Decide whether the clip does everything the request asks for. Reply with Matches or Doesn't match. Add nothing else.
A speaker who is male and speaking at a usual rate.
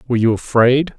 Matches